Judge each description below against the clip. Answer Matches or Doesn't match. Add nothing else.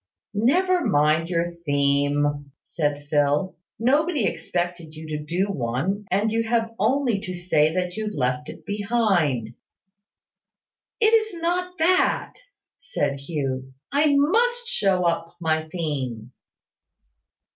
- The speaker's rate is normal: Doesn't match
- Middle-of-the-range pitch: Matches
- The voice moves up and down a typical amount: Doesn't match